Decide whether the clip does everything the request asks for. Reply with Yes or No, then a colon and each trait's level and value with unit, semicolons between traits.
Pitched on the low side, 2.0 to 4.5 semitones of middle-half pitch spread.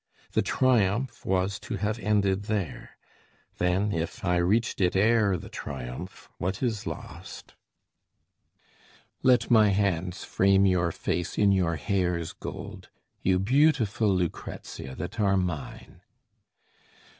Yes: very low, 95 Hz; average, 3.0 semitones